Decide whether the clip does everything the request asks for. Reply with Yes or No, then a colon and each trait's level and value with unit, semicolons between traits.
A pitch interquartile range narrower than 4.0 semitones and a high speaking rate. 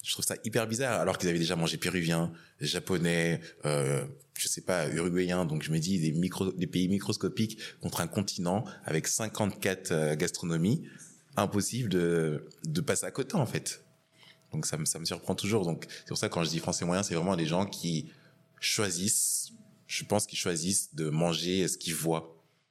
No: average, 3.4 semitones; average, 195 wpm